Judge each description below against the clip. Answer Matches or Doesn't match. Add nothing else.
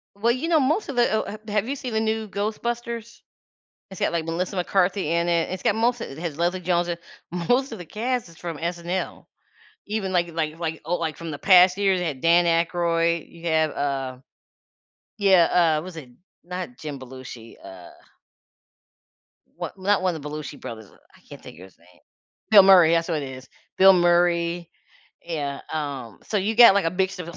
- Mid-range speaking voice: Matches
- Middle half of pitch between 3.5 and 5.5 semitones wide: Matches